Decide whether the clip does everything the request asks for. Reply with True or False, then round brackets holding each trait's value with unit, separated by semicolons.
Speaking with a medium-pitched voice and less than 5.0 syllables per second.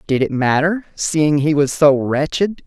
True (150 Hz; 4.1 syllables/s)